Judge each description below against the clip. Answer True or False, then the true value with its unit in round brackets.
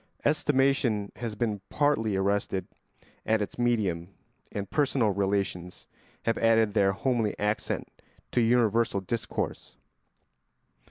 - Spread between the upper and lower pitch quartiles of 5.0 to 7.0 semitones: False (3.2 semitones)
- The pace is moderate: False (105 wpm)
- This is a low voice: True (110 Hz)